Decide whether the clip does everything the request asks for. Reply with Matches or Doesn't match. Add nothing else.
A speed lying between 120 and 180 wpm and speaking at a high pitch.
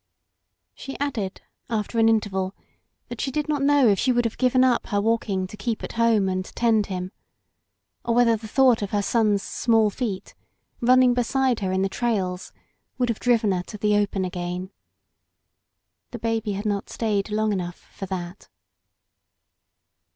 Matches